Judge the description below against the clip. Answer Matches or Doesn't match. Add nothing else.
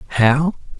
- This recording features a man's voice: Matches